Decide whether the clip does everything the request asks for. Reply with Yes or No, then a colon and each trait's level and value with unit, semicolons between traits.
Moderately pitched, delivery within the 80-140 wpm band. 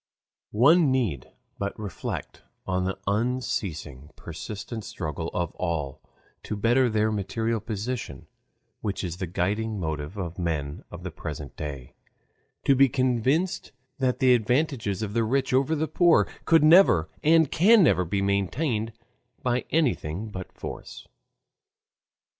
No: low, 105 Hz; slow, 135 wpm